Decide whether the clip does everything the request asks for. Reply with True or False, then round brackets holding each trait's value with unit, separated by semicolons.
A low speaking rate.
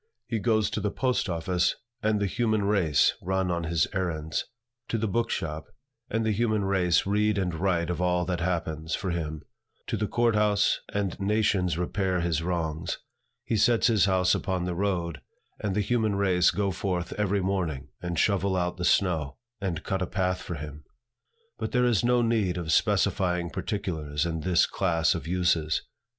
False (180 wpm)